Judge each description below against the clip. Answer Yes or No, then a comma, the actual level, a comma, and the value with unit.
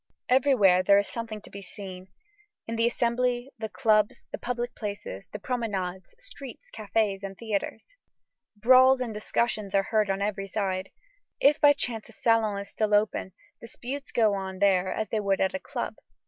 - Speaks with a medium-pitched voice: No, high, 215 Hz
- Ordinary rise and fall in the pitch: Yes, average, 3.3 semitones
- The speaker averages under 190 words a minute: Yes, average, 175 wpm